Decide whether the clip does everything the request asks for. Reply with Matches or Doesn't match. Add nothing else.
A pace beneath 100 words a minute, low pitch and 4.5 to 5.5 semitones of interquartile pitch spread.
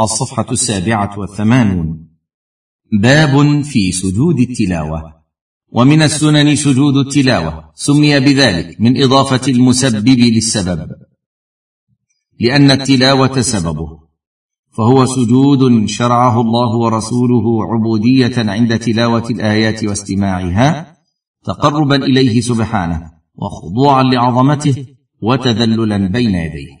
Matches